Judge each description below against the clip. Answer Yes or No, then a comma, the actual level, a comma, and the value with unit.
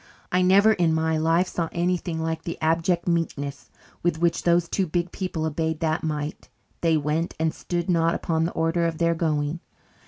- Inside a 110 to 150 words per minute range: No, average, 190 wpm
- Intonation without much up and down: Yes, narrow, 1.4 semitones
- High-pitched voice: No, medium, 165 Hz